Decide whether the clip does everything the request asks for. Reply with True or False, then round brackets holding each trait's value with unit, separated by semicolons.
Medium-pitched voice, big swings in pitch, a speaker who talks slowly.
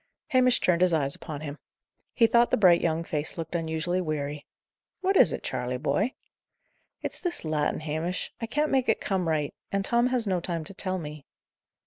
False (170 Hz; 6.3 semitones; 190 wpm)